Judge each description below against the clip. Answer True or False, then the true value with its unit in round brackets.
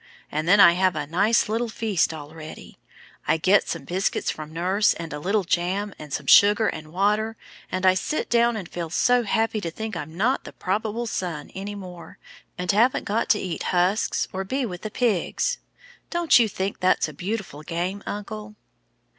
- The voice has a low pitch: False (195 Hz)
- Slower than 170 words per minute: False (190 wpm)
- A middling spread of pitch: True (4.0 semitones)